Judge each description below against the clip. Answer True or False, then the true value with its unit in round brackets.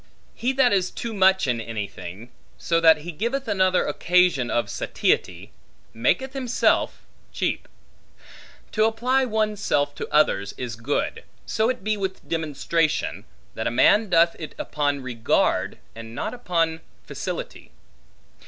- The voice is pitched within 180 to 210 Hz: False (170 Hz)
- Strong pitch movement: True (8.8 semitones)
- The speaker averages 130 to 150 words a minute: True (135 wpm)